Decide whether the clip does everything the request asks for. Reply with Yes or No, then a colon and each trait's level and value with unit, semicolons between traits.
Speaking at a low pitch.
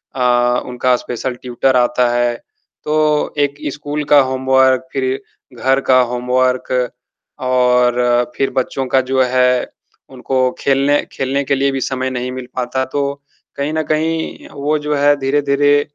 Yes: low, 130 Hz